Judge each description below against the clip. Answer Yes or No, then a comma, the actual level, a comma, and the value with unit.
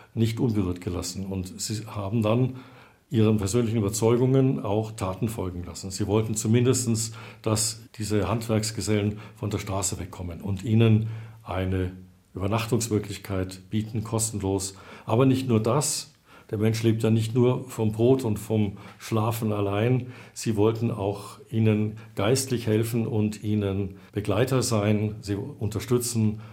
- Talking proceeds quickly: No, average, 130 wpm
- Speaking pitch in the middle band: No, low, 110 Hz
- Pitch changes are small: Yes, narrow, 2.2 semitones